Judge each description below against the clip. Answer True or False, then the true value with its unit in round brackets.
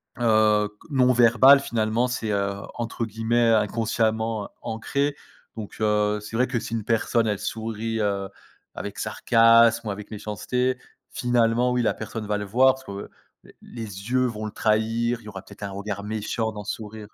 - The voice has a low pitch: True (110 Hz)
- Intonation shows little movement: True (2.1 semitones)